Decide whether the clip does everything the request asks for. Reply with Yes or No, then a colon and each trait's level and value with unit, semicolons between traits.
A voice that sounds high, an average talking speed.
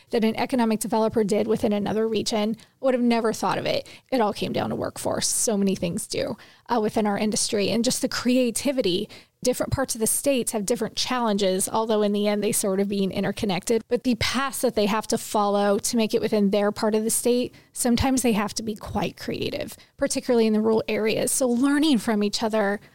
No: high, 220 Hz; fast, 215 wpm